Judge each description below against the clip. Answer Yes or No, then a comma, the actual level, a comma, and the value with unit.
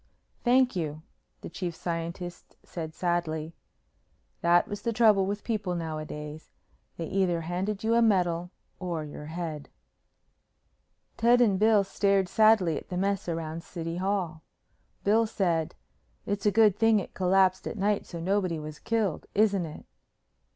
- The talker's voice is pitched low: No, medium, 185 Hz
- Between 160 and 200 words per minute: No, average, 150 wpm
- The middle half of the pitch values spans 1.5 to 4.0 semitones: Yes, average, 3.7 semitones